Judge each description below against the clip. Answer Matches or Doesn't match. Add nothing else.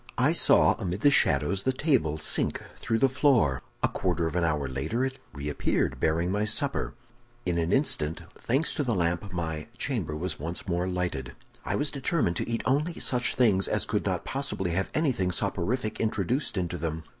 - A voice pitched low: Matches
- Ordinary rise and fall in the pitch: Doesn't match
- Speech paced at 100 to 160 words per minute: Doesn't match